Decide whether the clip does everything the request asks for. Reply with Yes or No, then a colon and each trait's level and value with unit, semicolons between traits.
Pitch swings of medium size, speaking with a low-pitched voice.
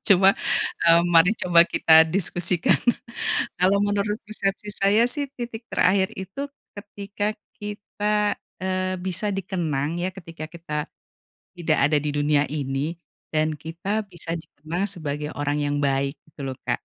No: average, 4.6 semitones; medium, 175 Hz